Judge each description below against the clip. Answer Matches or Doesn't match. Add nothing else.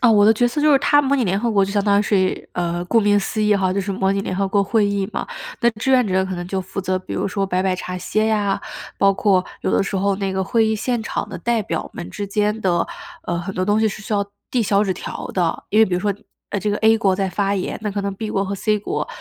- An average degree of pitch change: Doesn't match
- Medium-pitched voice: Doesn't match